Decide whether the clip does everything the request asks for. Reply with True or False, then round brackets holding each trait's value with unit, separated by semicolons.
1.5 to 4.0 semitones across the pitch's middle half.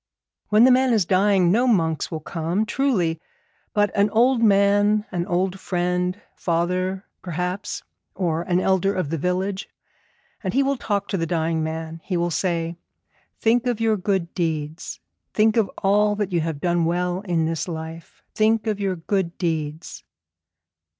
True (3.7 semitones)